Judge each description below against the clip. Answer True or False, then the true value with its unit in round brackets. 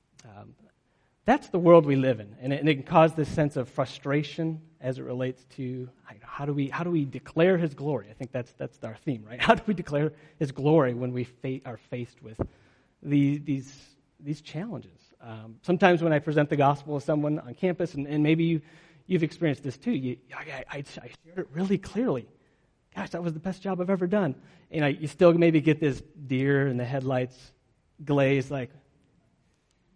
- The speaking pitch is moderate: True (145 Hz)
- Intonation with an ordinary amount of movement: True (3.8 semitones)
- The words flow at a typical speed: False (210 wpm)